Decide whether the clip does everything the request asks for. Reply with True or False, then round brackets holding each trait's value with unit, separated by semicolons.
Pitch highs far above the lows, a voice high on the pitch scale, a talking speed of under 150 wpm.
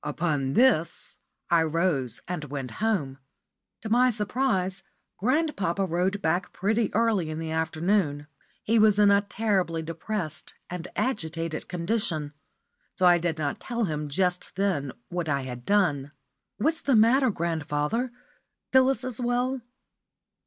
False (5.9 semitones; 180 Hz; 135 wpm)